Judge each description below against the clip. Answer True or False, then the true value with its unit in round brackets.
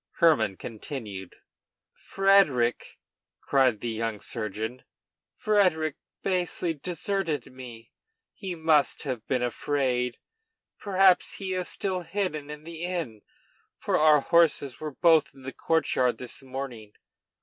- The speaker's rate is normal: False (115 wpm)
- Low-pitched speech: False (145 Hz)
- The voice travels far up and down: True (6.0 semitones)